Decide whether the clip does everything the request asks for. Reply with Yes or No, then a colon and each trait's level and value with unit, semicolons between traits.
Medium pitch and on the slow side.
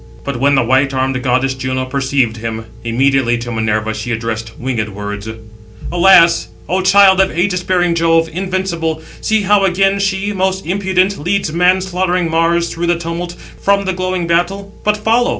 No: medium, 170 Hz; average, 170 wpm